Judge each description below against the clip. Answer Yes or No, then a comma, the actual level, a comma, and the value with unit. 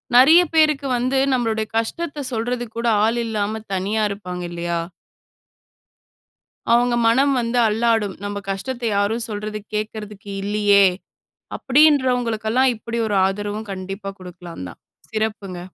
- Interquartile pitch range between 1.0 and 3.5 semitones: Yes, average, 3.2 semitones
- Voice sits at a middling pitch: No, high, 220 Hz